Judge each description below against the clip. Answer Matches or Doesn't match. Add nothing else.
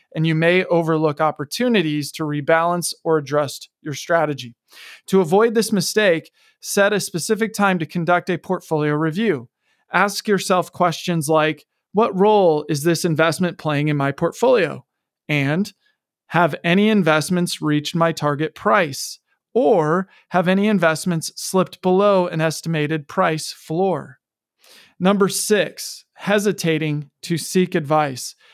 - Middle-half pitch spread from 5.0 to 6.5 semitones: Doesn't match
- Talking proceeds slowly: Matches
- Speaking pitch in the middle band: Matches